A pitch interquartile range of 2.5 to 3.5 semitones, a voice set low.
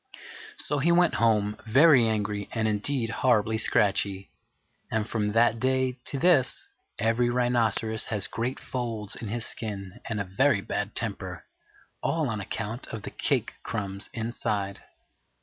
Yes: average, 2.9 semitones; low, 110 Hz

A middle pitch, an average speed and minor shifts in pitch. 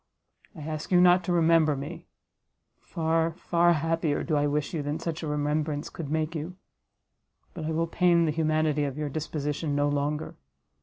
Yes: medium, 155 Hz; average, 175 wpm; narrow, 2.0 semitones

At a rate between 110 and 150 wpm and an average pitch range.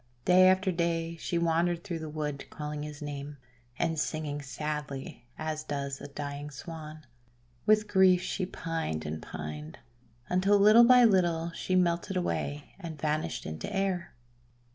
Yes: average, 145 wpm; average, 3.6 semitones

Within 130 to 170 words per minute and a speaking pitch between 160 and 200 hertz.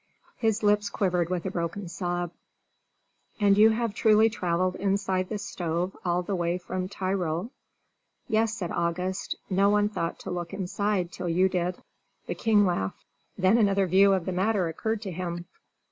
Yes: average, 165 wpm; medium, 185 Hz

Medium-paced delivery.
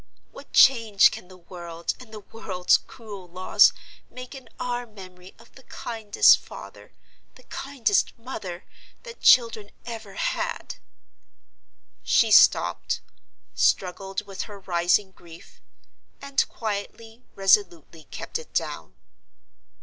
No: slow, 115 wpm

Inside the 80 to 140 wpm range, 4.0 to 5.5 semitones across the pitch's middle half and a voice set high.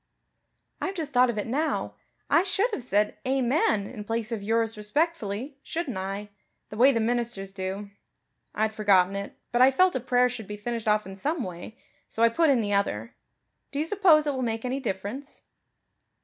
No: average, 190 wpm; average, 4.8 semitones; high, 230 Hz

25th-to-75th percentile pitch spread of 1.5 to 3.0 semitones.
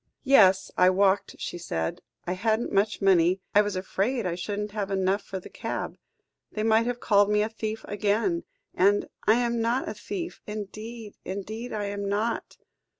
Yes: narrow, 2.4 semitones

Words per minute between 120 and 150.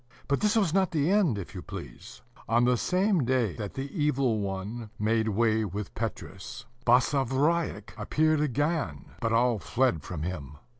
No: average, 160 wpm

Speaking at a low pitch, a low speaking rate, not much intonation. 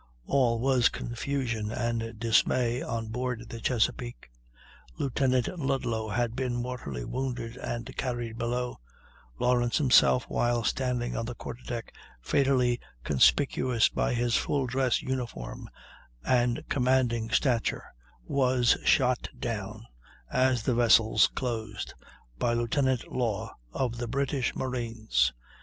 Yes: low, 120 Hz; slow, 115 wpm; narrow, 1.9 semitones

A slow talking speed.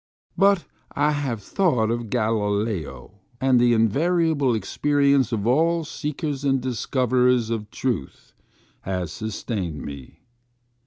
Yes: slow, 110 wpm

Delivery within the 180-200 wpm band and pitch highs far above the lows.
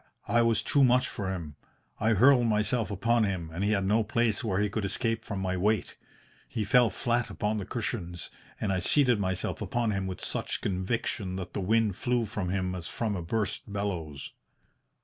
No: average, 195 wpm; average, 3.4 semitones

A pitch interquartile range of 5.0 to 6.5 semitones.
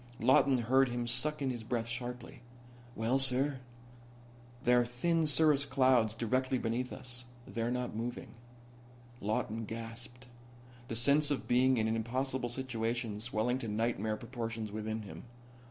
No: narrow, 2.4 semitones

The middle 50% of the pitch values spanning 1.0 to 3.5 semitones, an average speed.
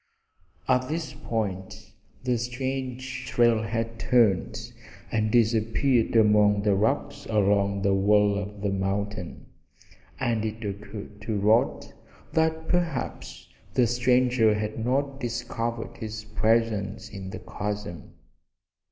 No: average, 3.1 semitones; slow, 115 wpm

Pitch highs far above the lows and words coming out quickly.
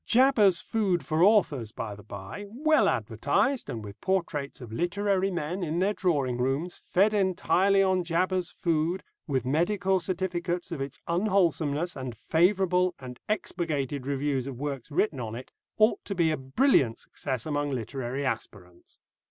No: wide, 6.0 semitones; average, 150 wpm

